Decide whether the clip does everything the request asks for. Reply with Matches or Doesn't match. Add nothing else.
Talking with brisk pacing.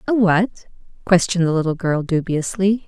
Doesn't match